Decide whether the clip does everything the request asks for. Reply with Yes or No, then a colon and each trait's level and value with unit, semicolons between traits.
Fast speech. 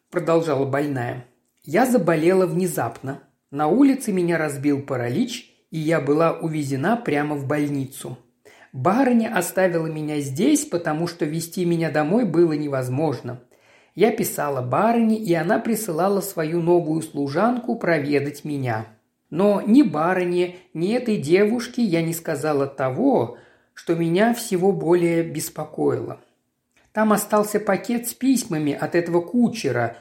No: average, 125 wpm